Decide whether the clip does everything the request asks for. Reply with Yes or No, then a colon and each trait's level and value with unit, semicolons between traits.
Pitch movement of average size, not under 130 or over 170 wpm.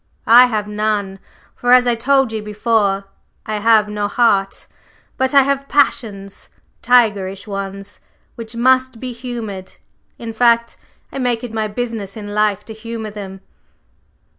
Yes: average, 3.0 semitones; average, 145 wpm